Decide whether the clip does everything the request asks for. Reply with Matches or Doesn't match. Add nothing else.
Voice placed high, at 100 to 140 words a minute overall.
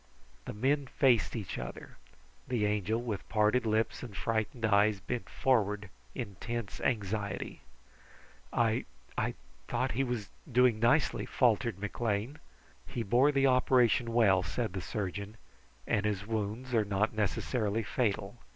Doesn't match